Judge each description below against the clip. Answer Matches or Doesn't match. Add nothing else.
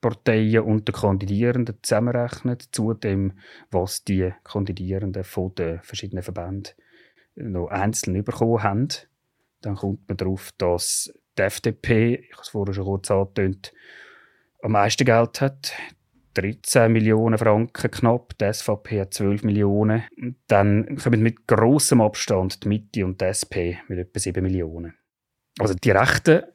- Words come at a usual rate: Matches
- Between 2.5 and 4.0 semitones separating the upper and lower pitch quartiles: Matches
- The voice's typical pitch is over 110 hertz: Doesn't match